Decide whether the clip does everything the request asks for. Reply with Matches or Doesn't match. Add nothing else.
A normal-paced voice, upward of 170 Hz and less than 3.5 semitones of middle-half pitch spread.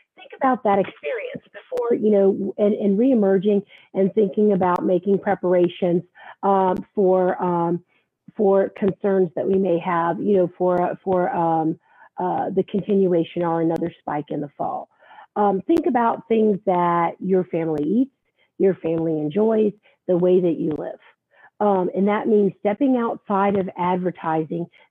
Matches